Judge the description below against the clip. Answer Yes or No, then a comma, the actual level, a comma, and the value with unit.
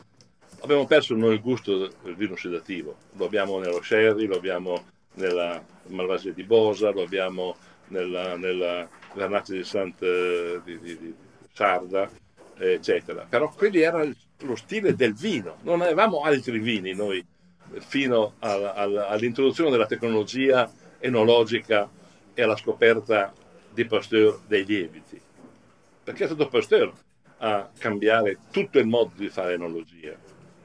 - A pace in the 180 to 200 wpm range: No, slow, 135 wpm